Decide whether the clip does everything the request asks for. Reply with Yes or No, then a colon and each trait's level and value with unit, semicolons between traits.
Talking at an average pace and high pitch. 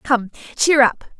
Yes: average, 150 wpm; very high, 255 Hz